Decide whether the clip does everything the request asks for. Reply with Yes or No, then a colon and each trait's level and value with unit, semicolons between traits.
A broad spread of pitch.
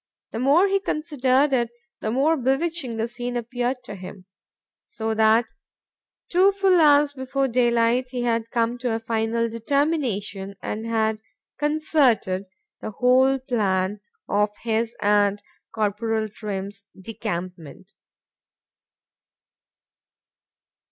No: average, 3.9 semitones